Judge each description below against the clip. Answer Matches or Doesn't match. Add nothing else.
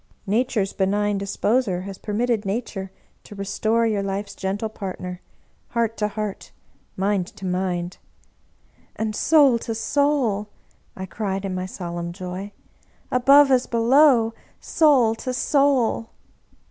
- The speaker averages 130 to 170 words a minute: Matches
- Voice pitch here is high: Matches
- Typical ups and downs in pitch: Matches